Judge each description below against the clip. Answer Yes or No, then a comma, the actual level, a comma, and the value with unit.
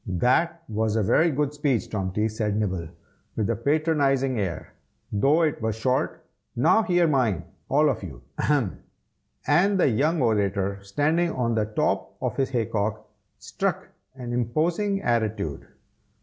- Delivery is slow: No, average, 150 wpm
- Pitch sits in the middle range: No, low, 120 Hz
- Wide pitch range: Yes, wide, 6.0 semitones